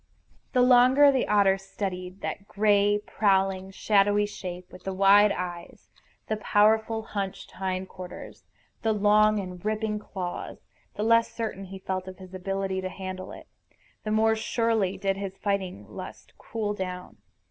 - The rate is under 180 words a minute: Yes, average, 150 wpm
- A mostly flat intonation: Yes, narrow, 2.2 semitones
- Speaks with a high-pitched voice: Yes, high, 195 Hz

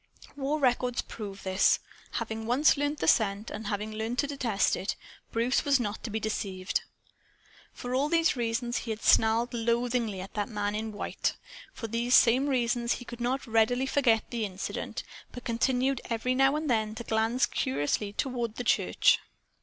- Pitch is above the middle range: Yes, high, 235 Hz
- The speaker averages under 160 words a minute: No, average, 175 wpm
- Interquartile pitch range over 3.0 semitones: No, average, 2.7 semitones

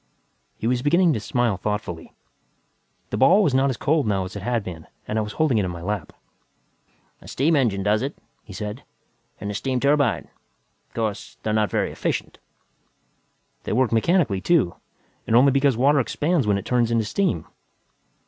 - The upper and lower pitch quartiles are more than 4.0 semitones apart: Yes, average, 5.0 semitones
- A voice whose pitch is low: Yes, low, 115 Hz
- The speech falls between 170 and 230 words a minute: Yes, average, 185 wpm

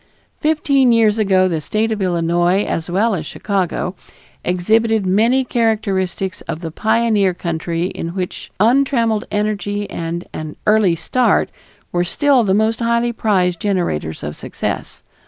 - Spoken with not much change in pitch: No, average, 4.2 semitones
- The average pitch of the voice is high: Yes, high, 200 Hz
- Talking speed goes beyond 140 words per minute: No, slow, 135 wpm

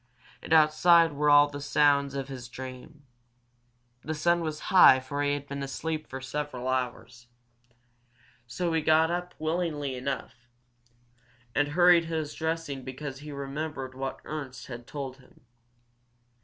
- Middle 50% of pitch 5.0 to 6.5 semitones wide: No, average, 3.0 semitones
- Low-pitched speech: No, medium, 145 Hz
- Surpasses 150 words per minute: No, average, 140 wpm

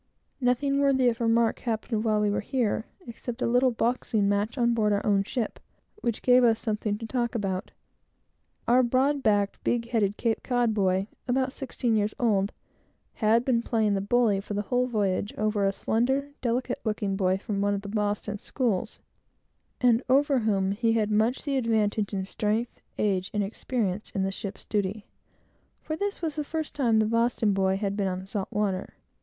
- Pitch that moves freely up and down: No, average, 3.2 semitones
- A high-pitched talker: Yes, high, 220 Hz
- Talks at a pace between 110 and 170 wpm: No, average, 185 wpm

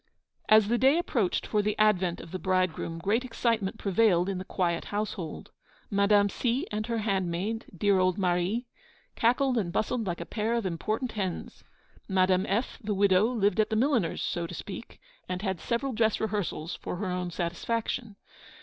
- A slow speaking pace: No, average, 175 wpm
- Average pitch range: Yes, average, 3.6 semitones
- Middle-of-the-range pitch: No, high, 205 Hz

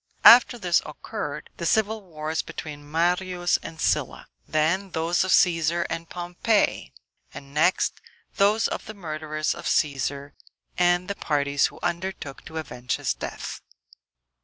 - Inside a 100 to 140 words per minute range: Yes, slow, 135 wpm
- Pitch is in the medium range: Yes, medium, 170 Hz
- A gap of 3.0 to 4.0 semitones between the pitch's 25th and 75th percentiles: Yes, average, 3.3 semitones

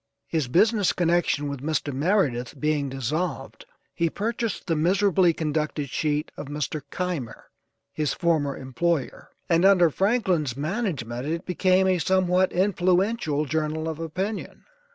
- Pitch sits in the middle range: Yes, medium, 165 Hz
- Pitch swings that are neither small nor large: Yes, average, 4.1 semitones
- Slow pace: Yes, slow, 130 wpm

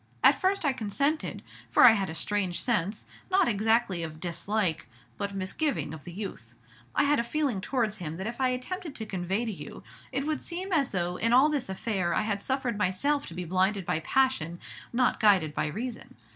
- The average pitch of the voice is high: Yes, high, 215 Hz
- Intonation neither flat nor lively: No, wide, 6.3 semitones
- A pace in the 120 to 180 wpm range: No, average, 200 wpm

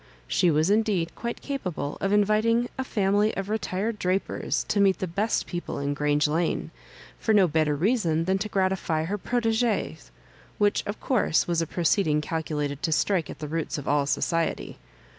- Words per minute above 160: Yes, average, 175 wpm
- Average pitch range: Yes, average, 4.9 semitones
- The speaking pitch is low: No, medium, 185 Hz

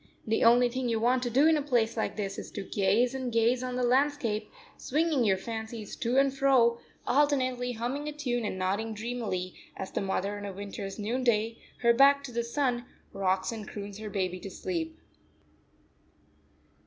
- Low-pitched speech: No, high, 235 Hz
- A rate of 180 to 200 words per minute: Yes, average, 185 wpm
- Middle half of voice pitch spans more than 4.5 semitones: No, average, 3.8 semitones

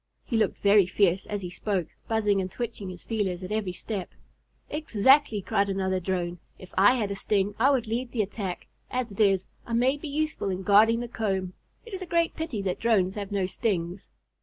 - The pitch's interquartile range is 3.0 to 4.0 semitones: Yes, average, 3.7 semitones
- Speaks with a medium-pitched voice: No, high, 205 Hz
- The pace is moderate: No, fast, 210 wpm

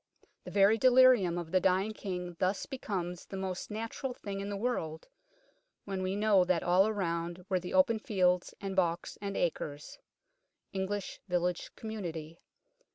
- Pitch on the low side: No, high, 190 Hz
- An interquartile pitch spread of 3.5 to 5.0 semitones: No, average, 3.0 semitones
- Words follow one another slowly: No, average, 160 wpm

